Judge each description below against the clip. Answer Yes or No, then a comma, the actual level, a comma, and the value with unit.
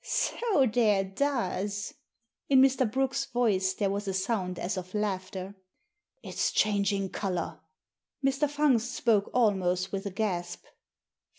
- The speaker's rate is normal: No, slow, 130 wpm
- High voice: Yes, high, 205 Hz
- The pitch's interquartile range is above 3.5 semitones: Yes, average, 4.6 semitones